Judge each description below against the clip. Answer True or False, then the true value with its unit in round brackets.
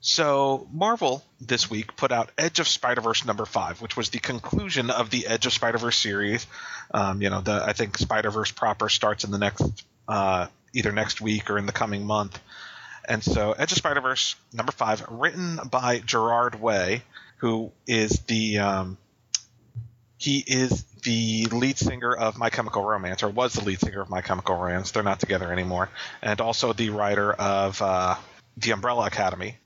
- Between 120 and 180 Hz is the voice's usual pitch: False (110 Hz)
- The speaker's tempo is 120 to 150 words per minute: False (185 wpm)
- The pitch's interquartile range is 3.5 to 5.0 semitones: False (2.9 semitones)